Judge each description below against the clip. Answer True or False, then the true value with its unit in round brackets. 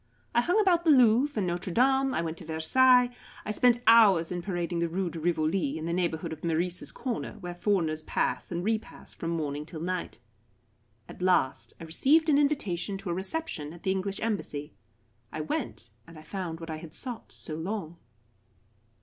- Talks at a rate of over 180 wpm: True (190 wpm)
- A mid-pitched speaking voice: True (180 Hz)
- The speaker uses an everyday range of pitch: False (5.8 semitones)